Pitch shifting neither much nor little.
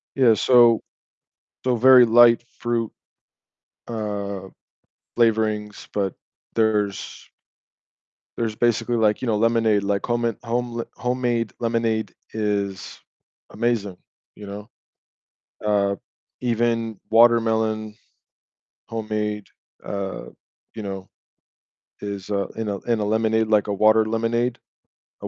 No: narrow, 2.1 semitones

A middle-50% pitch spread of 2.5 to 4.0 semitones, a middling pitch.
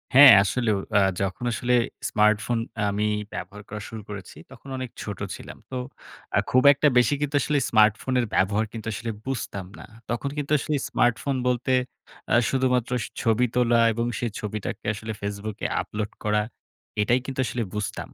No: average, 3.1 semitones; low, 115 Hz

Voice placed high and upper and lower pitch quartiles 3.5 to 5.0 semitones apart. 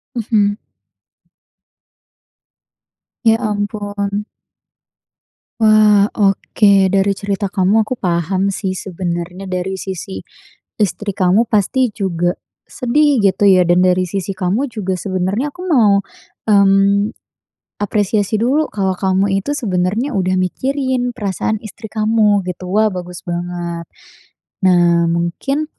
No: high, 200 Hz; average, 2.8 semitones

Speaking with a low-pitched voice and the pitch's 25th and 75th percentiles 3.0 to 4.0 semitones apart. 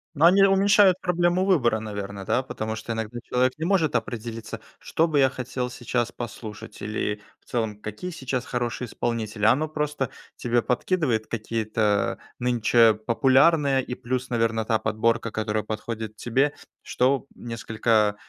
Yes: low, 120 Hz; average, 3.7 semitones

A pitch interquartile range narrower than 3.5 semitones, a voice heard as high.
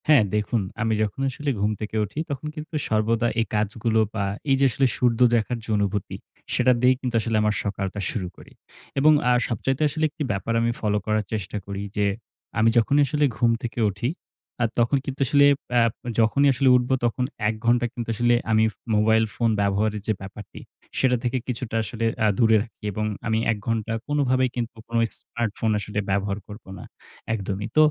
No: average, 3.0 semitones; low, 115 Hz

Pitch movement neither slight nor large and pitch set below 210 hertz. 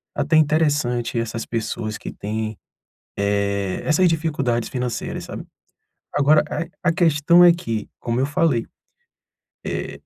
No: wide, 5.7 semitones; low, 135 Hz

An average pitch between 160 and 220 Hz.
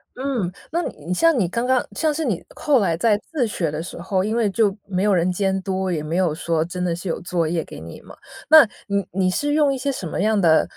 Yes: high, 190 Hz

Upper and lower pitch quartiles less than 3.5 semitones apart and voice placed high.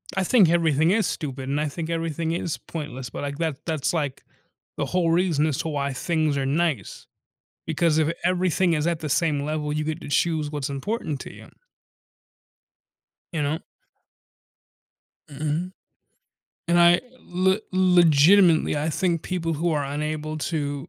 No: average, 2.8 semitones; medium, 155 Hz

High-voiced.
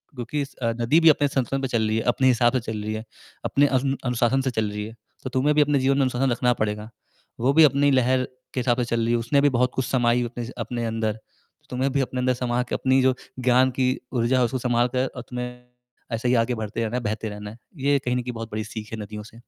No: low, 125 Hz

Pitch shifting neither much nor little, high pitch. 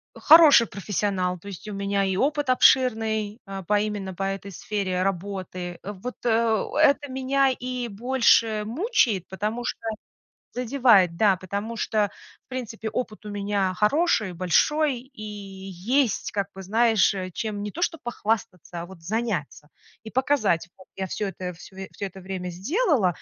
Yes: average, 4.2 semitones; high, 210 Hz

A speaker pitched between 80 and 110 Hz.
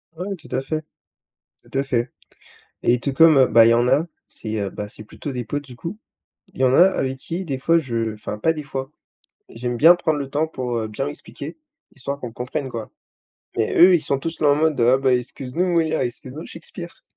No: low, 135 Hz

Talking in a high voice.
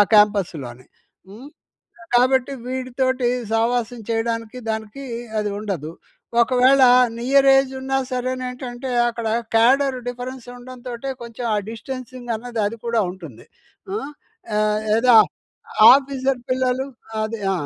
Yes: high, 245 Hz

